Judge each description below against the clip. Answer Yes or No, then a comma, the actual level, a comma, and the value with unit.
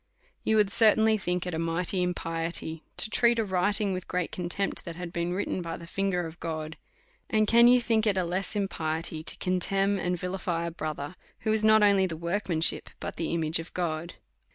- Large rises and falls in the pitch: No, average, 3.4 semitones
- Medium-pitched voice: Yes, medium, 180 Hz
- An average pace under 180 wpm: No, average, 200 wpm